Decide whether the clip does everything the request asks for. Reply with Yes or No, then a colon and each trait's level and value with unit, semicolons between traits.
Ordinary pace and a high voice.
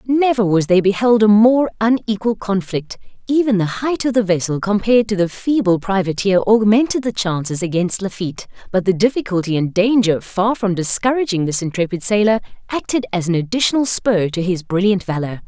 Yes: average, 170 wpm; high, 205 Hz